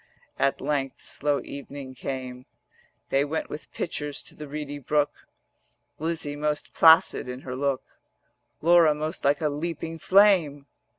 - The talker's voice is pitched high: No, medium, 145 Hz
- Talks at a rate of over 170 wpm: No, slow, 135 wpm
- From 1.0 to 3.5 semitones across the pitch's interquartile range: Yes, narrow, 2.4 semitones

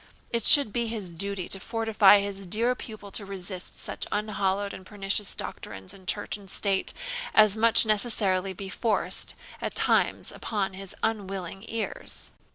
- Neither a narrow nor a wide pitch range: No, narrow, 2.1 semitones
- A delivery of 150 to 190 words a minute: Yes, average, 155 wpm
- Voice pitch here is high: Yes, high, 200 Hz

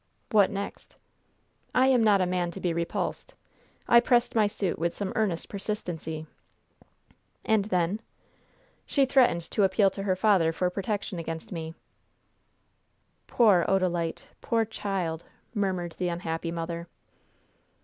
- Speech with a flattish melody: No, average, 3.7 semitones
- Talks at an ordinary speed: No, slow, 130 wpm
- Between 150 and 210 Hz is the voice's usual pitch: Yes, high, 190 Hz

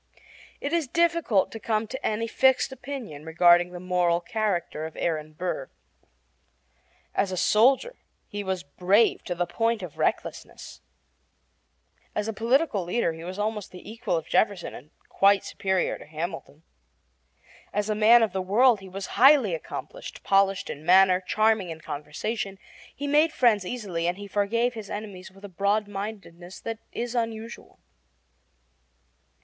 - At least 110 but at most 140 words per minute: No, average, 150 wpm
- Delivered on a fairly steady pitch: No, average, 4.3 semitones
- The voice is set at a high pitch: Yes, high, 200 Hz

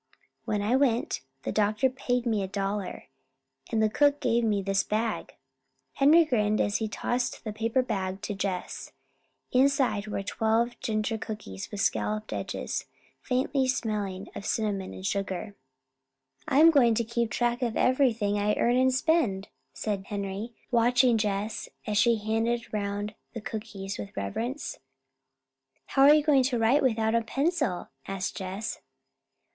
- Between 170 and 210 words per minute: No, average, 150 wpm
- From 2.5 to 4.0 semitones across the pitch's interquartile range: Yes, average, 3.4 semitones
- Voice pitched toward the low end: No, high, 220 Hz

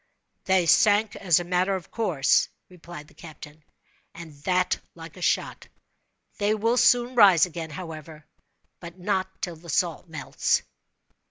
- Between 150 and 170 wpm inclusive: No, average, 140 wpm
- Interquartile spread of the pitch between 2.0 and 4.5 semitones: Yes, average, 3.0 semitones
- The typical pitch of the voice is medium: Yes, medium, 175 Hz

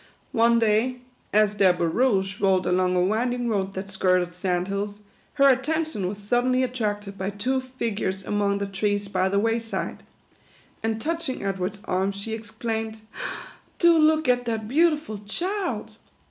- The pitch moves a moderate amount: Yes, average, 4.1 semitones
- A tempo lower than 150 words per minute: No, average, 160 wpm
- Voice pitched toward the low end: No, high, 215 Hz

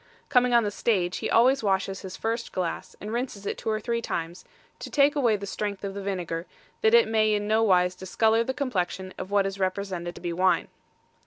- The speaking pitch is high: Yes, high, 200 Hz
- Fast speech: Yes, fast, 220 wpm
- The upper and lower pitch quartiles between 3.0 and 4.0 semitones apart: Yes, average, 3.6 semitones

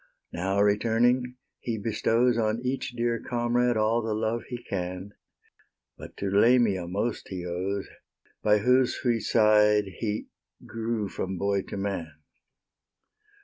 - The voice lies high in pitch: No, low, 110 Hz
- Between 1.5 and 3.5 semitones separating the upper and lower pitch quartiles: Yes, average, 3.1 semitones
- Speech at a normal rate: No, slow, 130 wpm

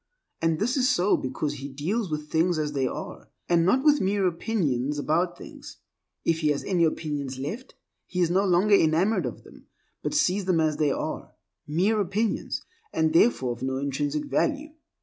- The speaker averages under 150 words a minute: No, average, 180 wpm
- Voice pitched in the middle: Yes, medium, 170 Hz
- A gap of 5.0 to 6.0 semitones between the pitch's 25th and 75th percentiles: Yes, wide, 5.4 semitones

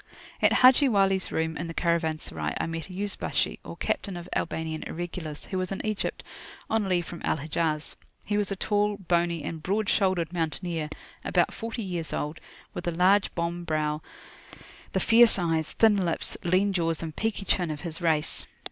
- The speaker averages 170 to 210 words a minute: Yes, average, 180 wpm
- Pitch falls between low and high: Yes, medium, 175 Hz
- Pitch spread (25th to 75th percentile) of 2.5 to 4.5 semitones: Yes, average, 3.5 semitones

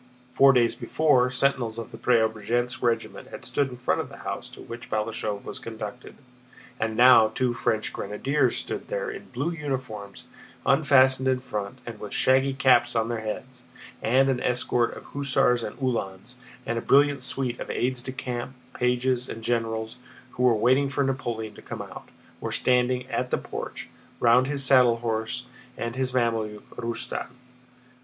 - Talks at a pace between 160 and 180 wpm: Yes, average, 170 wpm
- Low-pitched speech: Yes, low, 125 Hz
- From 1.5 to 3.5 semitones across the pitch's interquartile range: Yes, narrow, 2.4 semitones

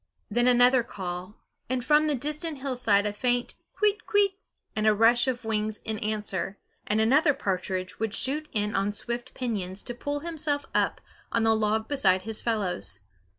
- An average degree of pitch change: Yes, average, 4.1 semitones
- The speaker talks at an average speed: Yes, average, 170 wpm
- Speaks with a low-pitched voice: No, high, 225 Hz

